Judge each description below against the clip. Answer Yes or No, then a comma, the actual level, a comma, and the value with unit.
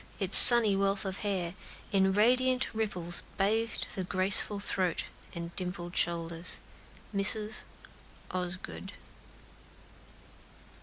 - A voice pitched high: Yes, high, 195 Hz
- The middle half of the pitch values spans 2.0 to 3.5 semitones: Yes, average, 2.8 semitones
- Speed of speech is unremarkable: No, slow, 95 wpm